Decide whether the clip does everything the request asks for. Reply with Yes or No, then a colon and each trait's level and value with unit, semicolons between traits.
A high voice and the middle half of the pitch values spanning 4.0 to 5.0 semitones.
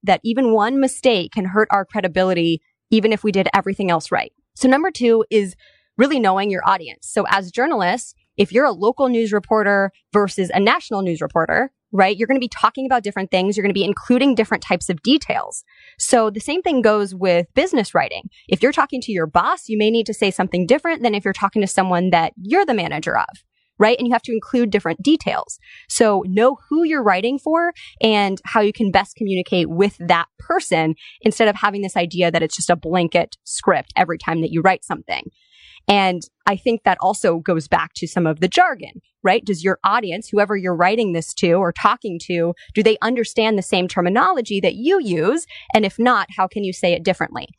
Yes: high, 205 Hz; average, 4.3 semitones